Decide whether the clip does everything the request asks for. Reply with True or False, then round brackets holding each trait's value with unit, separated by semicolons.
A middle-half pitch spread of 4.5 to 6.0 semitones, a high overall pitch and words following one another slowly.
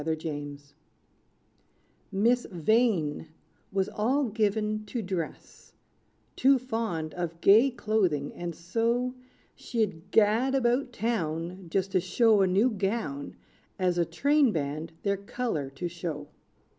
True (5.6 semitones; 195 Hz; 120 wpm)